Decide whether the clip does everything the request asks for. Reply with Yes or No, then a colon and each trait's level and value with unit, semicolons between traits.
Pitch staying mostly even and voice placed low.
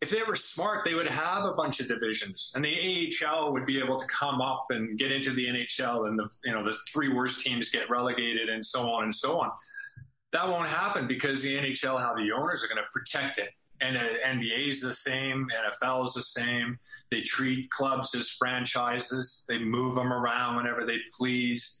Yes: narrow, 2.1 semitones; low, 130 Hz